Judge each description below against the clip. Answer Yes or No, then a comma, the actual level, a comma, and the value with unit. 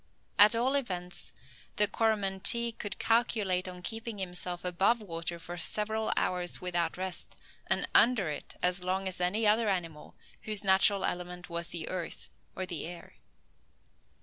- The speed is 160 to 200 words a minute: No, average, 150 wpm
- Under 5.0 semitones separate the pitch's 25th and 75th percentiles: Yes, average, 3.2 semitones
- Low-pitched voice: No, medium, 185 Hz